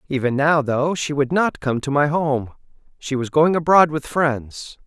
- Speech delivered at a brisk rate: No, average, 195 wpm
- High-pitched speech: No, medium, 145 Hz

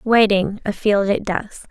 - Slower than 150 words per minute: Yes, average, 140 wpm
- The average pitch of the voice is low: No, high, 205 Hz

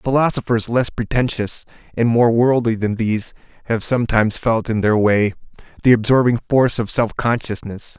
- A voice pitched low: Yes, low, 115 Hz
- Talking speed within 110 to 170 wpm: Yes, average, 150 wpm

